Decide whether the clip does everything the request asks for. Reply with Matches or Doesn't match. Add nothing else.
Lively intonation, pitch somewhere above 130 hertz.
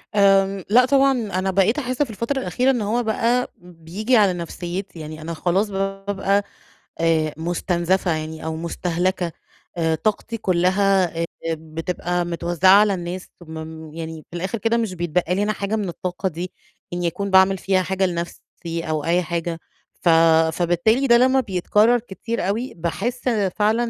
Doesn't match